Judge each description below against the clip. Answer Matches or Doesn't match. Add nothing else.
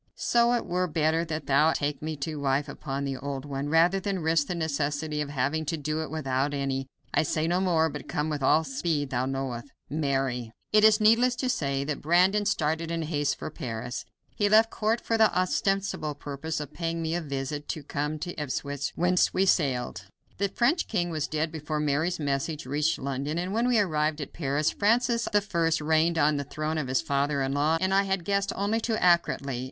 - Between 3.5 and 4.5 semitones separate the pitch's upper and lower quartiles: Matches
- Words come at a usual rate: Doesn't match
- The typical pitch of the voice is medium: Matches